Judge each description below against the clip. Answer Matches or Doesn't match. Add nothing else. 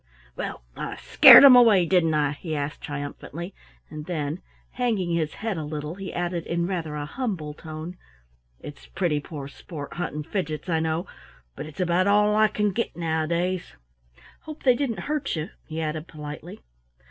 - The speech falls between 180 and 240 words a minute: Doesn't match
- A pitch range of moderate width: Matches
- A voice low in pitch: Doesn't match